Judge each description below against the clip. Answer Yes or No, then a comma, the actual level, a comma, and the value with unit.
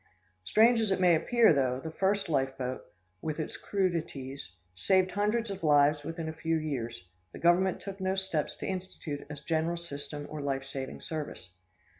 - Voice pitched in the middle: Yes, medium, 160 Hz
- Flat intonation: No, average, 4.9 semitones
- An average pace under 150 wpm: No, average, 175 wpm